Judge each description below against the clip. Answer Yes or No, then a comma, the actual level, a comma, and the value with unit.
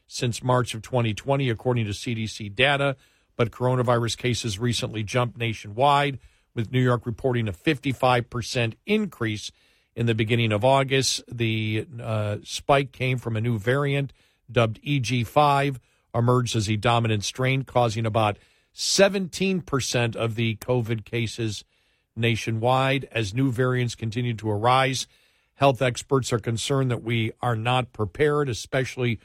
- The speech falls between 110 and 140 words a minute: Yes, slow, 135 wpm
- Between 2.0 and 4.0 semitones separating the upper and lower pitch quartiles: Yes, narrow, 2.5 semitones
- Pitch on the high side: No, low, 120 Hz